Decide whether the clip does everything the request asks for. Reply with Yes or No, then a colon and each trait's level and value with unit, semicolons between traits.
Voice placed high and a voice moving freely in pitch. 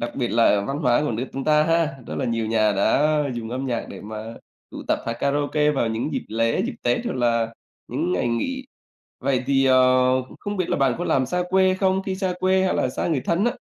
No: low, 135 Hz; wide, 6.2 semitones